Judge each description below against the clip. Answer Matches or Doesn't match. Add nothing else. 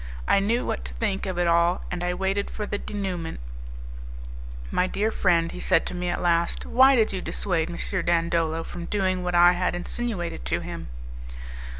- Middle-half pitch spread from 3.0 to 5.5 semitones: Doesn't match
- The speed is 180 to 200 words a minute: Matches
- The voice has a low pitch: Doesn't match